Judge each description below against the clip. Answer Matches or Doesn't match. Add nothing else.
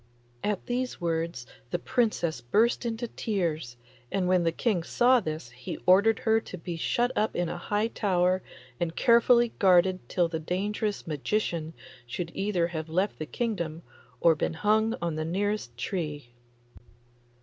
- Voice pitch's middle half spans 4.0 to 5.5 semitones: Matches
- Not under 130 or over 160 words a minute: Matches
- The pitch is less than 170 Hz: Doesn't match